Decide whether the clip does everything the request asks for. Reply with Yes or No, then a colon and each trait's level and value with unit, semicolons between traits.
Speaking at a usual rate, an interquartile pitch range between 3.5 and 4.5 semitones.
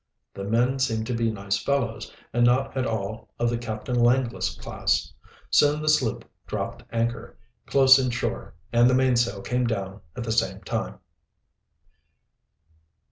No: average, 150 wpm; narrow, 2.4 semitones